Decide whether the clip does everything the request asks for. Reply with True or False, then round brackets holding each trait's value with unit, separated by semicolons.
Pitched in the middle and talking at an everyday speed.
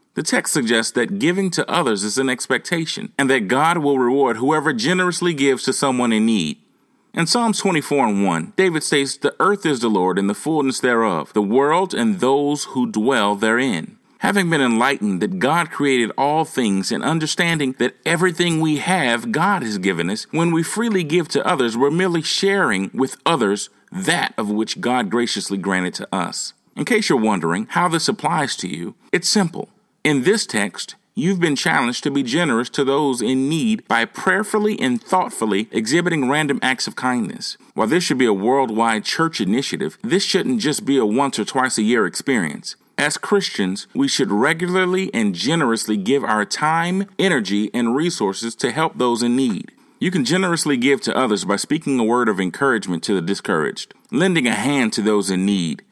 True (145 Hz; 185 wpm)